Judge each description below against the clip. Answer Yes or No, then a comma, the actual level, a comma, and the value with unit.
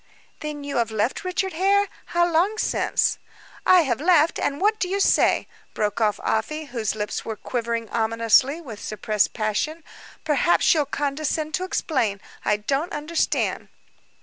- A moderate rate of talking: Yes, average, 150 wpm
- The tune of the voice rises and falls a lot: Yes, wide, 7.2 semitones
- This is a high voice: Yes, very high, 285 Hz